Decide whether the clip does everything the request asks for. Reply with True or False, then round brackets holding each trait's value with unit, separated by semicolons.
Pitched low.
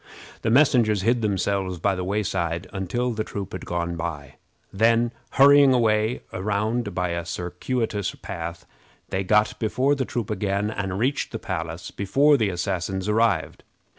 True (100 Hz)